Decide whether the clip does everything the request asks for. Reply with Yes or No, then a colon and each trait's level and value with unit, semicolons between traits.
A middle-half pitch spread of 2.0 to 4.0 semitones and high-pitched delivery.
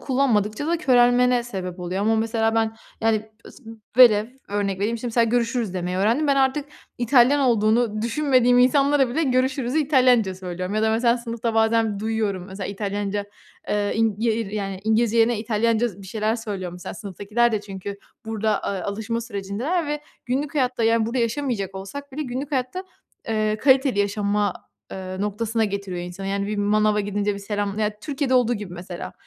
Yes: average, 3.4 semitones; high, 220 Hz